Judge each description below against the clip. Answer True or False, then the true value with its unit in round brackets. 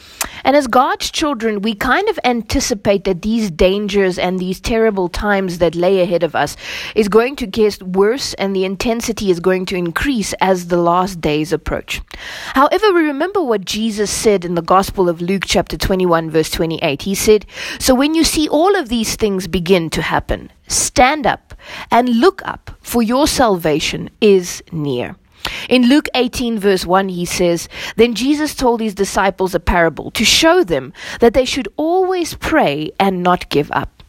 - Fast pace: False (180 wpm)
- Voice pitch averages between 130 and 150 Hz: False (205 Hz)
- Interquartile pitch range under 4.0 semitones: False (5.2 semitones)